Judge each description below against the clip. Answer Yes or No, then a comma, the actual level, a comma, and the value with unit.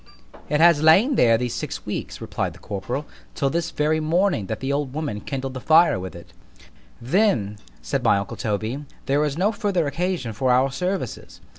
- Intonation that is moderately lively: No, wide, 5.7 semitones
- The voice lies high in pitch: No, medium, 145 Hz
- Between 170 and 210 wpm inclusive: Yes, average, 185 wpm